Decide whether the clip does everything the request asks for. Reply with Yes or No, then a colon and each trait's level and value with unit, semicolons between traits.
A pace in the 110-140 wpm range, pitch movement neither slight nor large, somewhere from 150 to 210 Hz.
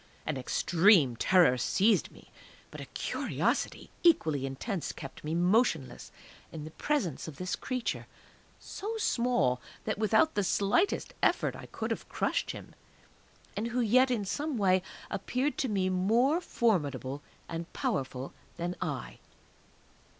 No: slow, 135 wpm; wide, 7.7 semitones; high, 190 Hz